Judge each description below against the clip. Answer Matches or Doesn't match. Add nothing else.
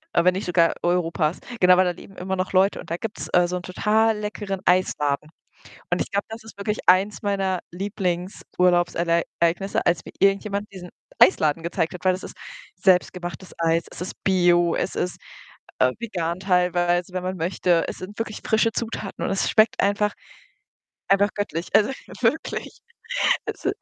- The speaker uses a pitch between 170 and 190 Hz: Matches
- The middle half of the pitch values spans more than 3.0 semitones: Doesn't match